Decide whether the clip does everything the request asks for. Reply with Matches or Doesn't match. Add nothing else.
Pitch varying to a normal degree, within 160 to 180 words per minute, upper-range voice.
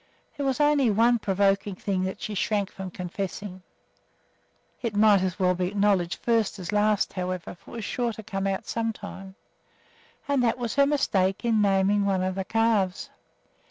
Matches